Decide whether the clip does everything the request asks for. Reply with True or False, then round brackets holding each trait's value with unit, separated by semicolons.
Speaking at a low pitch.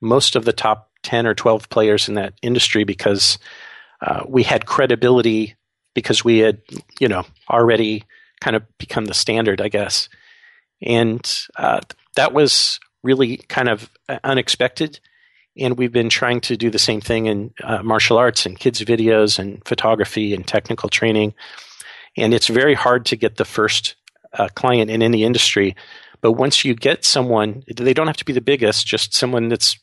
True (115 Hz)